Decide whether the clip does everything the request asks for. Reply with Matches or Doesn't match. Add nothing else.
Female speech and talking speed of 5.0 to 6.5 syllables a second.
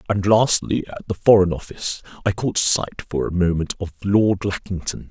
Doesn't match